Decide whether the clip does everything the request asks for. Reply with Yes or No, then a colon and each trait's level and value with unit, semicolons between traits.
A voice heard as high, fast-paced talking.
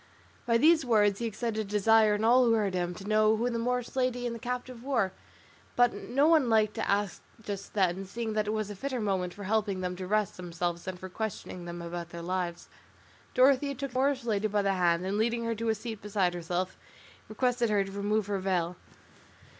Yes: high, 215 Hz; fast, 220 wpm